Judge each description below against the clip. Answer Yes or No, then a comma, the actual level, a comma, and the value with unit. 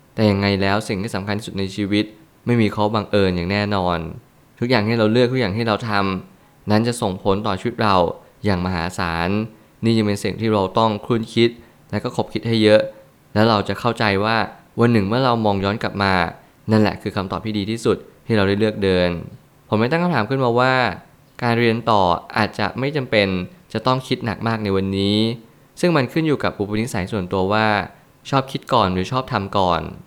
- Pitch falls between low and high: No, low, 110 Hz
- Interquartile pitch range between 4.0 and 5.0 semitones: No, average, 3.2 semitones